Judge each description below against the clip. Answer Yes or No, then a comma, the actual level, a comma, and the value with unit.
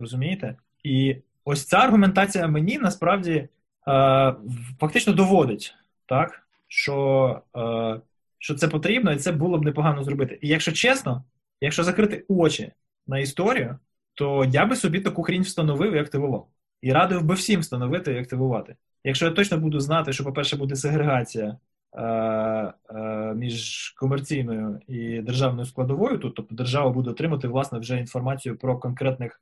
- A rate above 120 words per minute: Yes, average, 145 wpm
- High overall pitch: No, low, 135 Hz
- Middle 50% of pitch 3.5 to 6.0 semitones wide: Yes, average, 4.6 semitones